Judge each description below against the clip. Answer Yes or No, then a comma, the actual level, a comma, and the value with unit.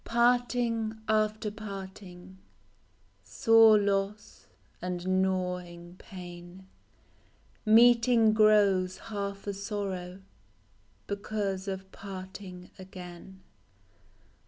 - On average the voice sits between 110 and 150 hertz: No, high, 195 Hz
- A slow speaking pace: Yes, slow, 70 wpm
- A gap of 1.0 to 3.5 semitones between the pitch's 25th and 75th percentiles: Yes, narrow, 2.6 semitones